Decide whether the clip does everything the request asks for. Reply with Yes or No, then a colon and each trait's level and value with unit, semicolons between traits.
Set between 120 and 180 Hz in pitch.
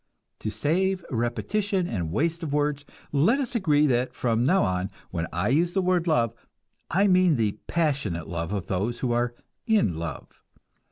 Yes: medium, 140 Hz